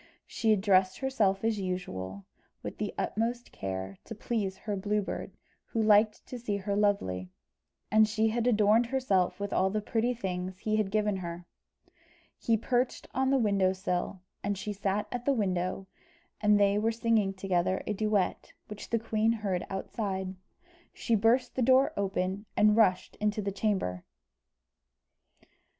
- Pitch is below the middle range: No, high, 205 Hz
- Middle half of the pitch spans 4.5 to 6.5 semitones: No, average, 2.8 semitones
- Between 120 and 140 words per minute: No, average, 160 wpm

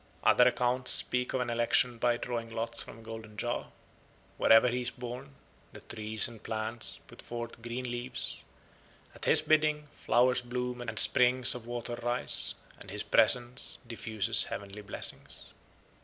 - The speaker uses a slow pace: No, average, 155 wpm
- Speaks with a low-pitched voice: Yes, low, 120 Hz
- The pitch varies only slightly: Yes, narrow, 1.7 semitones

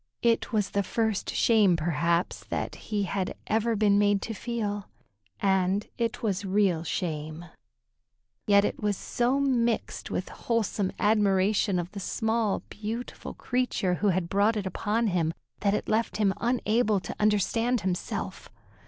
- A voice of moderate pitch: No, high, 205 Hz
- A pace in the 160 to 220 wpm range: No, average, 145 wpm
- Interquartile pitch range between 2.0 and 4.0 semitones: Yes, average, 3.0 semitones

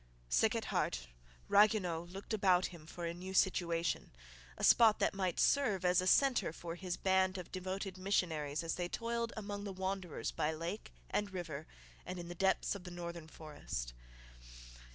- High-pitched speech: No, medium, 180 Hz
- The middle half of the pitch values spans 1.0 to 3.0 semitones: Yes, average, 2.7 semitones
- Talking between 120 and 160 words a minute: No, average, 175 wpm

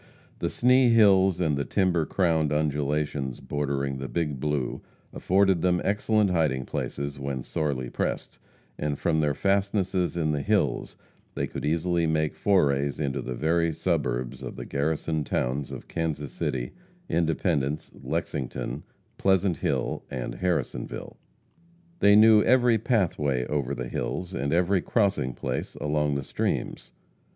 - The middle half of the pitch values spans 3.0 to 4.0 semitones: No, average, 4.8 semitones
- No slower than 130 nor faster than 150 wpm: Yes, average, 140 wpm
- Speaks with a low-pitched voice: Yes, very low, 80 Hz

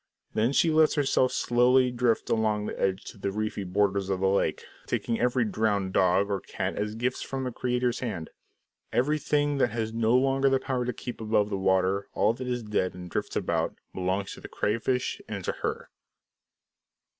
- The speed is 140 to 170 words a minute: No, average, 190 wpm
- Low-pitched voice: Yes, low, 110 Hz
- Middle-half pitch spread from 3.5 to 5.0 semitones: Yes, average, 4.1 semitones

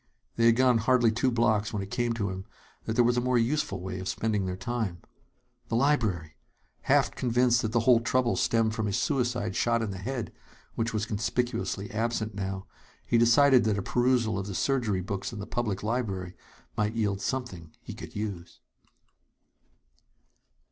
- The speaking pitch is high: No, low, 115 Hz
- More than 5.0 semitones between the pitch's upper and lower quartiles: No, average, 3.4 semitones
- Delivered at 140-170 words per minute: No, average, 180 wpm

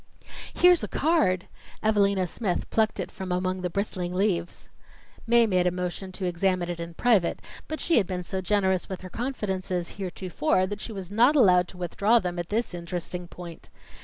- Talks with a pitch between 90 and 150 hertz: No, medium, 185 Hz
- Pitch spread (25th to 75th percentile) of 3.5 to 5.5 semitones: No, average, 2.7 semitones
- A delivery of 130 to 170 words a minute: No, average, 185 wpm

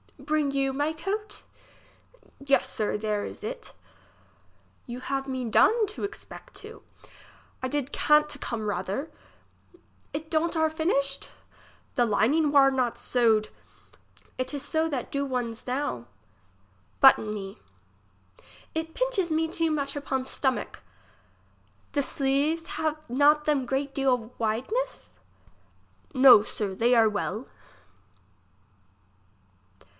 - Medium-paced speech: No, slow, 120 wpm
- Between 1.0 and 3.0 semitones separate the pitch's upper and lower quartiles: No, average, 4.4 semitones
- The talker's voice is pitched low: No, very high, 275 Hz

